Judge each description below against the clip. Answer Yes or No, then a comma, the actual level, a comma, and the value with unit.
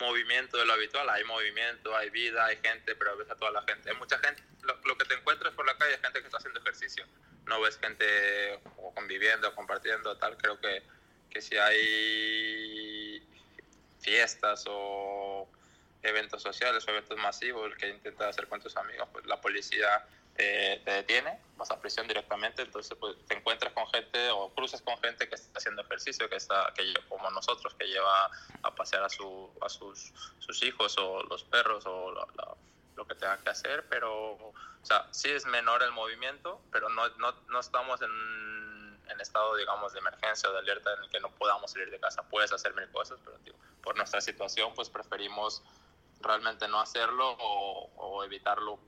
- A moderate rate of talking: Yes, average, 190 wpm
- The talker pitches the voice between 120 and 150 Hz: No, low, 110 Hz